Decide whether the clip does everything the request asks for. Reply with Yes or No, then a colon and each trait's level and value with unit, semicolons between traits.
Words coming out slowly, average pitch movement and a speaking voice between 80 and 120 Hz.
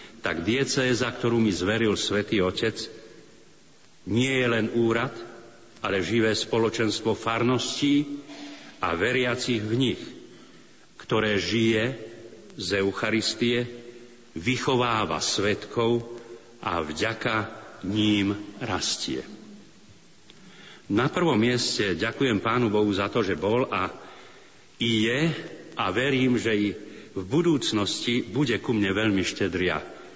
No: slow, 105 wpm; narrow, 2.3 semitones; low, 115 Hz